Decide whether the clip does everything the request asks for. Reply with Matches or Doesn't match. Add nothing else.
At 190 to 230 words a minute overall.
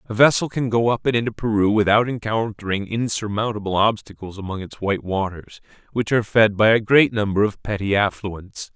Doesn't match